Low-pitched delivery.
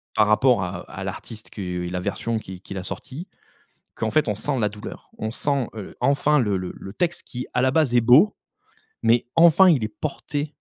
Yes: low, 115 Hz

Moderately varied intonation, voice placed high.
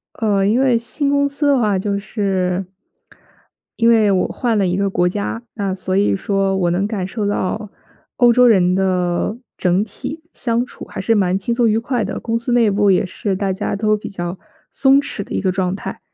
Yes: average, 3.5 semitones; high, 205 Hz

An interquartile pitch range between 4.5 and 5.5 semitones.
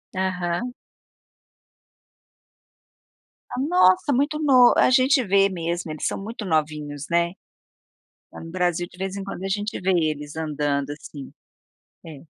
Yes: average, 5.1 semitones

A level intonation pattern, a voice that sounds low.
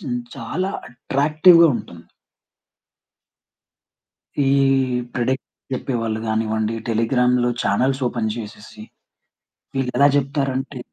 No: average, 3.4 semitones; low, 125 Hz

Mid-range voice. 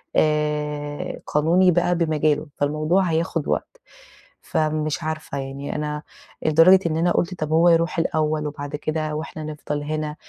Yes: medium, 155 Hz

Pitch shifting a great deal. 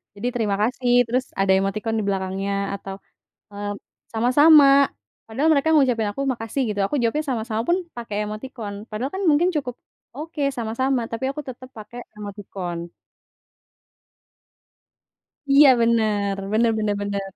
No: average, 4.2 semitones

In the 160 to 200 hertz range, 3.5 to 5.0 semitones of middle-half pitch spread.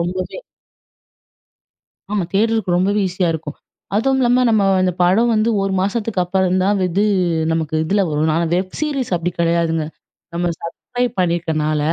Yes: medium, 185 Hz; average, 4.1 semitones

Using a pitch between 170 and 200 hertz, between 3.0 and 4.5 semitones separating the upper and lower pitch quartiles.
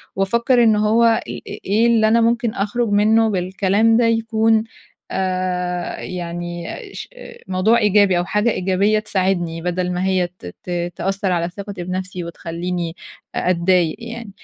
Yes: high, 190 Hz; average, 3.6 semitones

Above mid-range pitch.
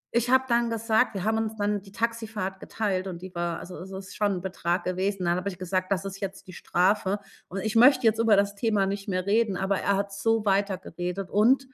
Yes: high, 200 Hz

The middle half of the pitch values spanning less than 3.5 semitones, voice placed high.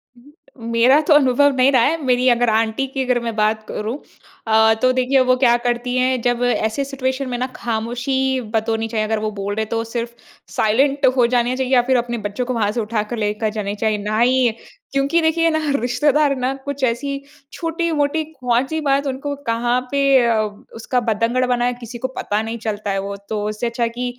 Yes: average, 3.1 semitones; high, 245 Hz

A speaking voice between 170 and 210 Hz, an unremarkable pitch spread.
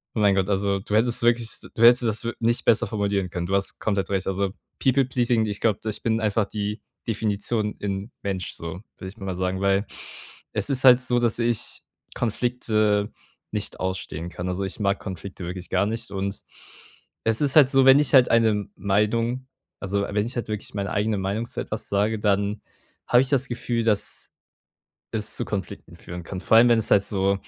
No: low, 105 Hz; average, 3.0 semitones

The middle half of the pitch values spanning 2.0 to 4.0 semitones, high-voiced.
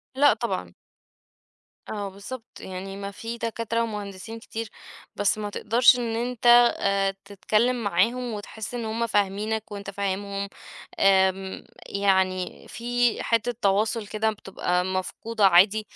Yes: average, 2.8 semitones; high, 210 Hz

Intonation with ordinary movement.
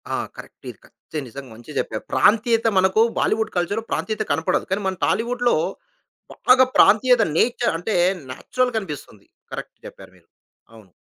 No: wide, 6.6 semitones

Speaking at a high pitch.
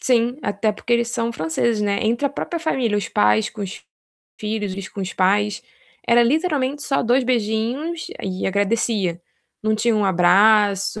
Yes: high, 215 Hz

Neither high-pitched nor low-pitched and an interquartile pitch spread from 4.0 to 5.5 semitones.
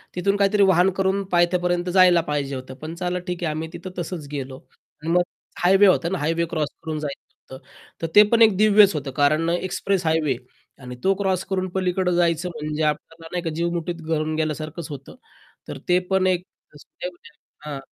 No: medium, 170 Hz; average, 3.3 semitones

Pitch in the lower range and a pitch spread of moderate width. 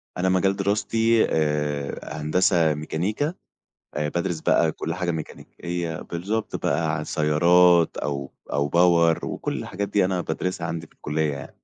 Yes: very low, 85 Hz; average, 3.2 semitones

